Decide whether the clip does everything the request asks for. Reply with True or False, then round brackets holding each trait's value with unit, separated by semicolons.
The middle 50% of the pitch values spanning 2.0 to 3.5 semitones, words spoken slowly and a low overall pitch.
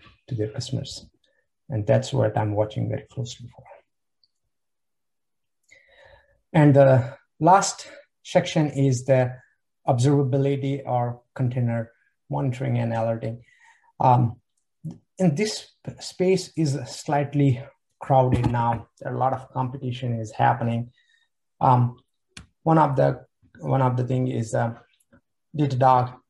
True (2.9 semitones; 110 wpm; 130 Hz)